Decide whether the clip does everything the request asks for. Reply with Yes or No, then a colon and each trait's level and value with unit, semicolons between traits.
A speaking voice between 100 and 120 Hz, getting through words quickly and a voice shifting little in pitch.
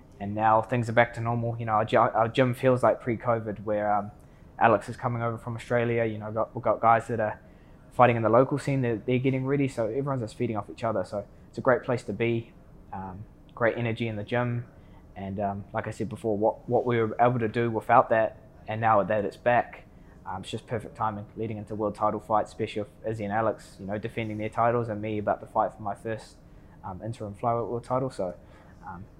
Yes: low, 110 Hz; fast, 240 wpm; narrow, 2.2 semitones